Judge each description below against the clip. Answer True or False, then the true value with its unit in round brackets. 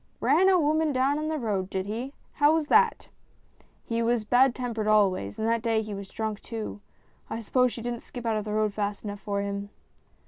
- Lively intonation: False (3.8 semitones)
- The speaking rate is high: True (235 wpm)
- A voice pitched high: True (225 Hz)